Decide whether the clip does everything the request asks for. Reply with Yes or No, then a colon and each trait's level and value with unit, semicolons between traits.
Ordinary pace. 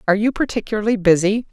Yes: average, 160 wpm